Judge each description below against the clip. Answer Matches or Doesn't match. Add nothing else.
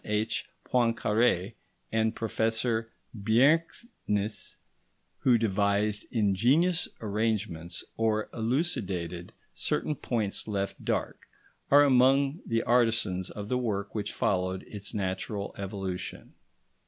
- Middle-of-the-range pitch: Doesn't match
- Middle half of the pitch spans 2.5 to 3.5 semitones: Matches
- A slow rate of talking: Matches